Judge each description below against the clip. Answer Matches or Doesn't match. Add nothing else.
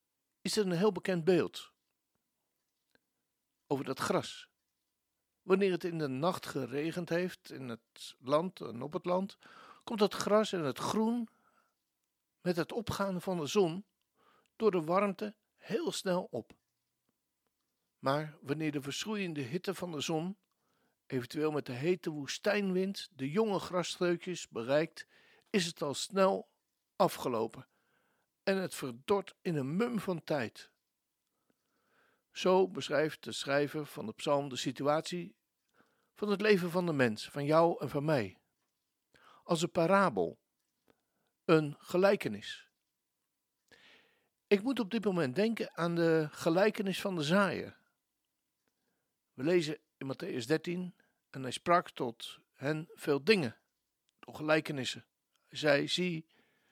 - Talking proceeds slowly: Matches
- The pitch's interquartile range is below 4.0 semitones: Doesn't match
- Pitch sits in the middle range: Matches